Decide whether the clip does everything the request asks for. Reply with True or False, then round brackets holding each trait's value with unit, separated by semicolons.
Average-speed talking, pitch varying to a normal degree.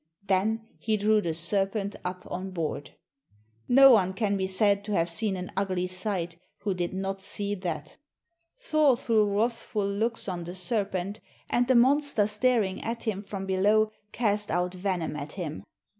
True (165 wpm; 3.0 semitones)